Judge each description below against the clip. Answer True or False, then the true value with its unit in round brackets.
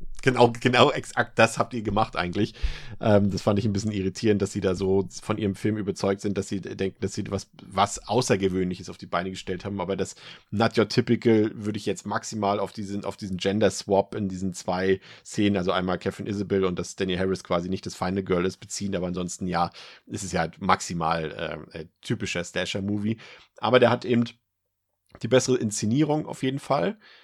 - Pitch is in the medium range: False (100 Hz)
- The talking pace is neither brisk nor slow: False (200 wpm)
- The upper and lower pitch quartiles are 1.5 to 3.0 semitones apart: True (2.7 semitones)